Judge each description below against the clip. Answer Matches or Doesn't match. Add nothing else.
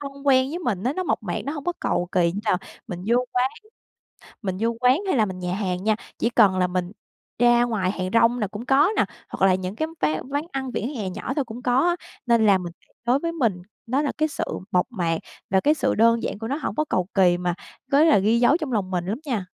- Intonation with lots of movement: Matches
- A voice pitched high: Matches